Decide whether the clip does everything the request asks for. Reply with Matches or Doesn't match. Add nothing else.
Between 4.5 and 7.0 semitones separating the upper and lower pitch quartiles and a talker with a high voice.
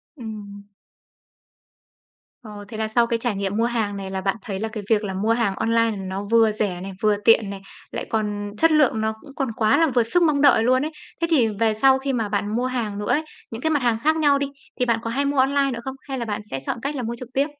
Doesn't match